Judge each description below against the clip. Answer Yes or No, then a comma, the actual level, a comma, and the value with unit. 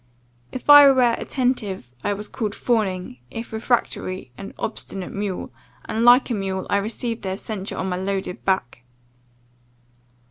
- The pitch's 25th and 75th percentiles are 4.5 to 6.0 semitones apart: No, average, 3.7 semitones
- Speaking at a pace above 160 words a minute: No, average, 145 wpm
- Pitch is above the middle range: Yes, high, 205 Hz